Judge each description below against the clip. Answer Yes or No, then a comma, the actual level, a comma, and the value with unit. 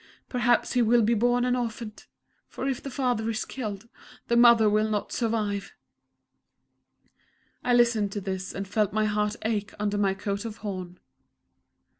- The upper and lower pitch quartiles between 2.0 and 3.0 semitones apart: Yes, narrow, 2.6 semitones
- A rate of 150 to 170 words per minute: Yes, average, 160 wpm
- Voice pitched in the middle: No, high, 220 Hz